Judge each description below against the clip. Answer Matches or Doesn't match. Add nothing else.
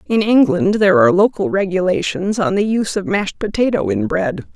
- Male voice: Doesn't match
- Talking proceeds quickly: Doesn't match